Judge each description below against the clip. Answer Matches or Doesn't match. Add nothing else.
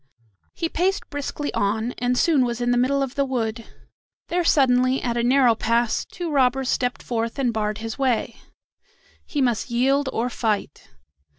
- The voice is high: Matches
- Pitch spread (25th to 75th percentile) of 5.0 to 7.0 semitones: Doesn't match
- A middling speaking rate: Matches